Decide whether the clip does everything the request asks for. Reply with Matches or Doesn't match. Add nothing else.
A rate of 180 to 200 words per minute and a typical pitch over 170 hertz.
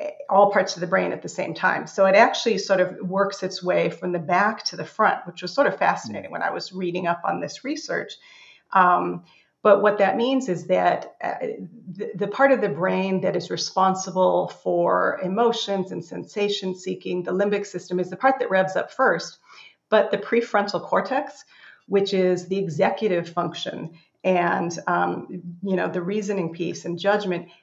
Matches